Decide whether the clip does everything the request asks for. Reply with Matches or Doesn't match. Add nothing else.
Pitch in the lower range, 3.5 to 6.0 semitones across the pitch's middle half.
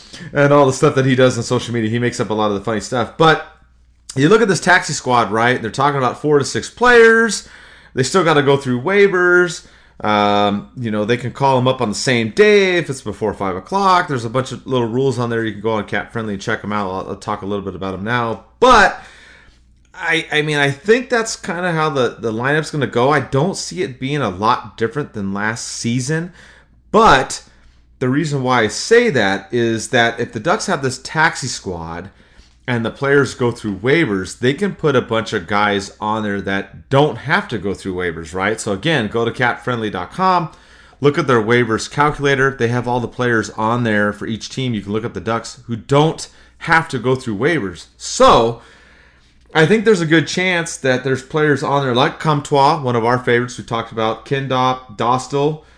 Matches